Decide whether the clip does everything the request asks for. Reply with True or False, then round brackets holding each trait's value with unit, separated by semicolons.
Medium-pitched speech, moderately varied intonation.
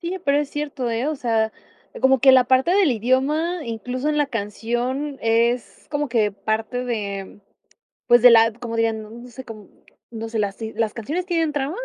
False (245 Hz; 4.2 semitones)